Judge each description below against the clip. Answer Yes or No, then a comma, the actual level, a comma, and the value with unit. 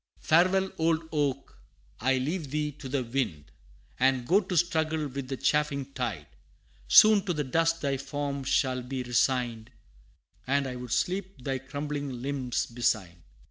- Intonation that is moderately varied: Yes, average, 3.6 semitones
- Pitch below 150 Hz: Yes, medium, 140 Hz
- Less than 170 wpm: Yes, average, 150 wpm